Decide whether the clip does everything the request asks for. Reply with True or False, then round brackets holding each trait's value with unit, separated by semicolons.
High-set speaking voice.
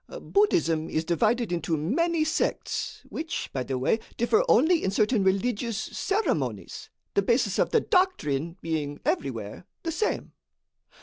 True (200 Hz)